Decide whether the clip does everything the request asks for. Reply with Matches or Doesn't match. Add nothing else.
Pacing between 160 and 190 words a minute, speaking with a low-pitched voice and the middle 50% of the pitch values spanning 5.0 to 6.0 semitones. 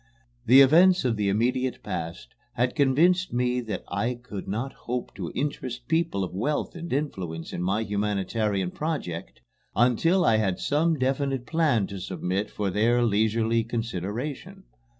Doesn't match